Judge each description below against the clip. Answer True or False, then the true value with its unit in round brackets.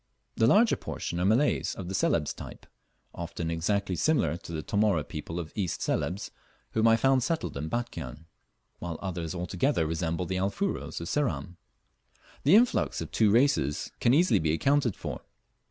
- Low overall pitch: True (95 Hz)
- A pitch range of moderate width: False (6.9 semitones)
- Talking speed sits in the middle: True (165 wpm)